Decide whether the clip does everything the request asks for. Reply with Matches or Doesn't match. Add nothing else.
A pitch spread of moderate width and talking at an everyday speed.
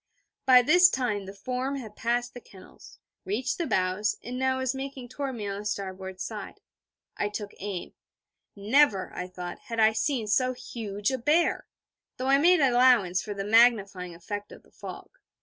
Matches